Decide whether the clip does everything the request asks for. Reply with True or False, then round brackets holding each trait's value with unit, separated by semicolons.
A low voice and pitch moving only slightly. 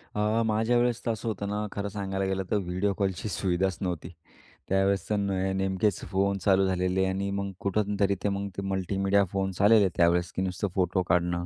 True (95 Hz; 1.5 semitones)